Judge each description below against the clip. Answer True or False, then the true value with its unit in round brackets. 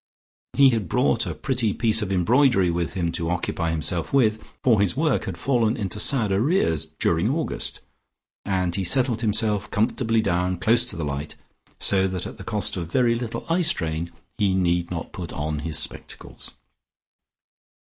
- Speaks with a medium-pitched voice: False (100 Hz)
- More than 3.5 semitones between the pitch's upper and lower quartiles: True (5.3 semitones)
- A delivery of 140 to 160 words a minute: False (170 wpm)